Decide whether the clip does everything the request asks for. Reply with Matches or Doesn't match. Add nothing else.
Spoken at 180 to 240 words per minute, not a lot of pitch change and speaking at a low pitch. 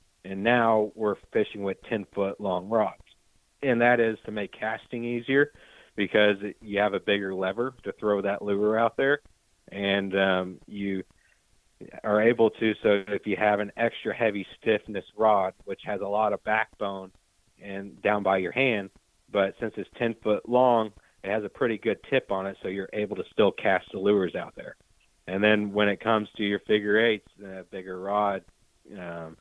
Matches